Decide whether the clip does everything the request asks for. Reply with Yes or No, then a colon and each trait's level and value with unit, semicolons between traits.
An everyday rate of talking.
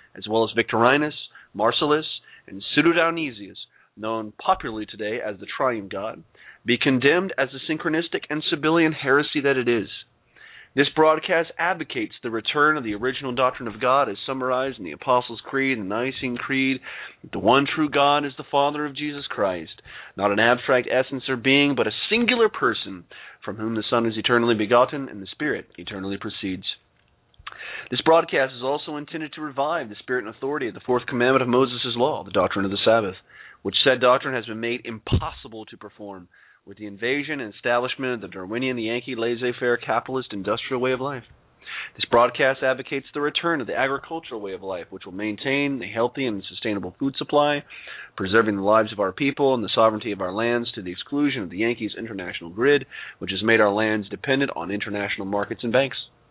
Yes: average, 190 wpm